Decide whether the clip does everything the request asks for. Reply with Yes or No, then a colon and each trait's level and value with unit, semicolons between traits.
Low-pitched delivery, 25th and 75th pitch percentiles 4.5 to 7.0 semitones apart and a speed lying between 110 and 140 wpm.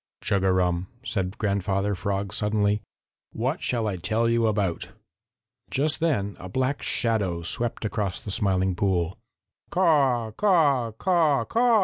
Yes: low, 105 Hz; average, 5.3 semitones; slow, 135 wpm